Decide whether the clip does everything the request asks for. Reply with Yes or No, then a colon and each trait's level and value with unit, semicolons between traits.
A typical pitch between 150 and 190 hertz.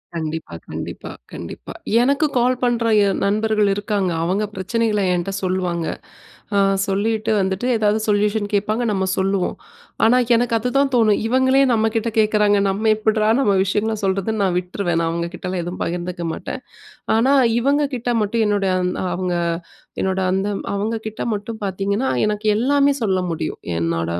No: high, 205 Hz